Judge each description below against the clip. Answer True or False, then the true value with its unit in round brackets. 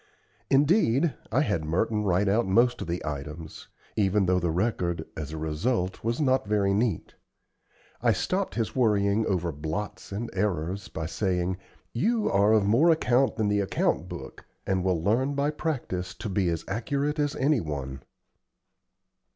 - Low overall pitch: True (100 Hz)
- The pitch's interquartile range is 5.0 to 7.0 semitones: True (5.5 semitones)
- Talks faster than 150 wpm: True (160 wpm)